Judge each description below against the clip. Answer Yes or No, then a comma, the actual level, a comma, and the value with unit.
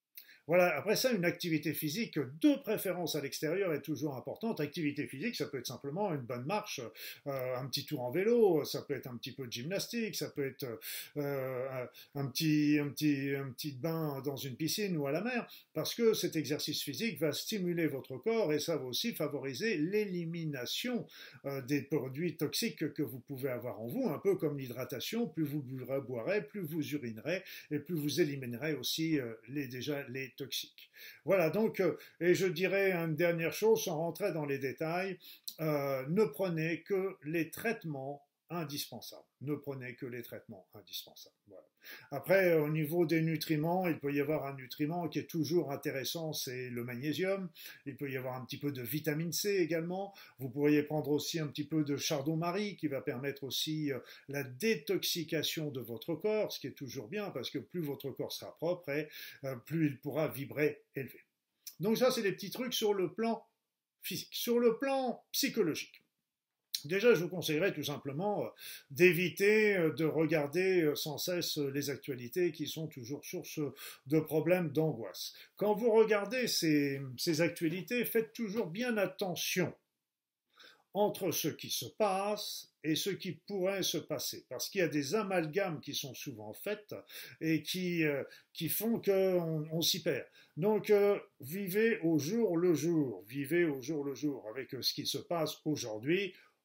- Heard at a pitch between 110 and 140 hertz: No, medium, 155 Hz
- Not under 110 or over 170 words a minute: No, average, 180 wpm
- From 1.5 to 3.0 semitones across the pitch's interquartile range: No, average, 4.8 semitones